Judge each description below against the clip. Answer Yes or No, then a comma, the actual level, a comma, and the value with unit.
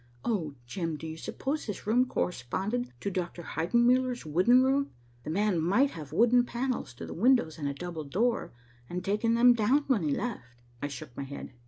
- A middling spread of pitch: No, wide, 7.5 semitones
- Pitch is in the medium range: No, high, 200 Hz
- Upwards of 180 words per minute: Yes, average, 190 wpm